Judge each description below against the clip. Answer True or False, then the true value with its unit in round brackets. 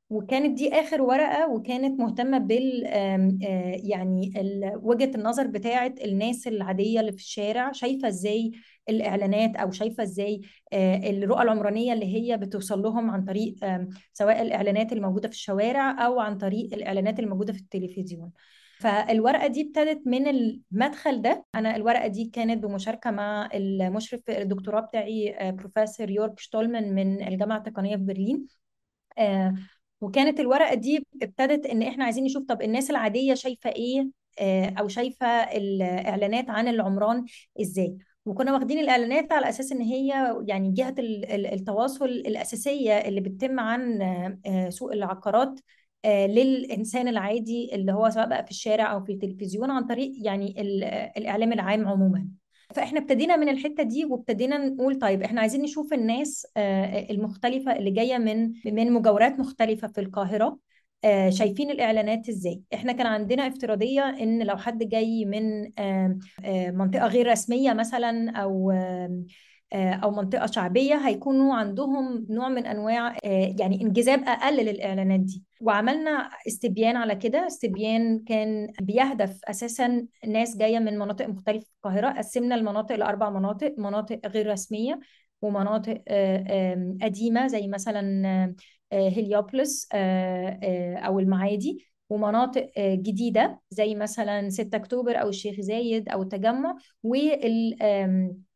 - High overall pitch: True (220 Hz)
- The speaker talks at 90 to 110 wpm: False (125 wpm)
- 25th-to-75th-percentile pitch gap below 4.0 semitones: True (3.5 semitones)